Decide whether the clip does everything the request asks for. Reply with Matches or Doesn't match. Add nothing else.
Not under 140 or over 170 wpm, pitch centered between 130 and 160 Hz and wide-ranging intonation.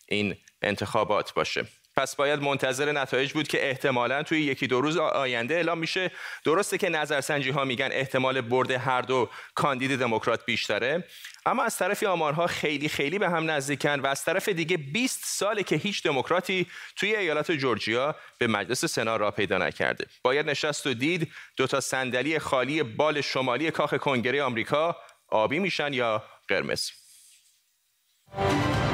Doesn't match